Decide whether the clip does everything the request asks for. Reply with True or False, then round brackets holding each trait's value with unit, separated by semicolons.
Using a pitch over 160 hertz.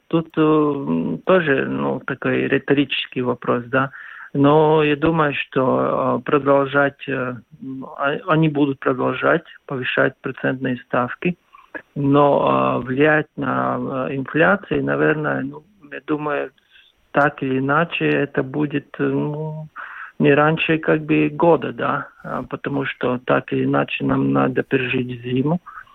False (145 Hz)